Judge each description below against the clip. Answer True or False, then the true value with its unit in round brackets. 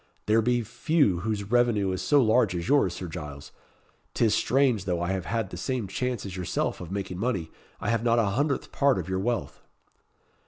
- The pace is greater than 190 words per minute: True (200 wpm)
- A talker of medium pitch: False (105 Hz)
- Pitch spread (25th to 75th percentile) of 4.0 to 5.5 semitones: True (4.7 semitones)